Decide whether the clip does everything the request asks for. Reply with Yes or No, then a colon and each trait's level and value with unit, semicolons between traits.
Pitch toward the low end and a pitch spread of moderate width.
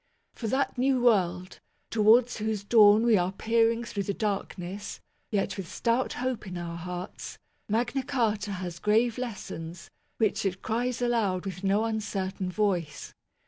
No: high, 210 Hz; average, 3.7 semitones